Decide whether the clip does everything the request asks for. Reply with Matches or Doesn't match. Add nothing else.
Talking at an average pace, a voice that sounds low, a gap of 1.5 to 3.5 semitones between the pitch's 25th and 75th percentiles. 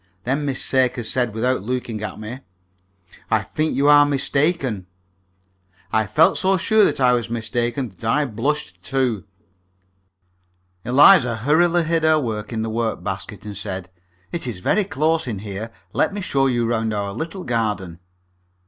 Doesn't match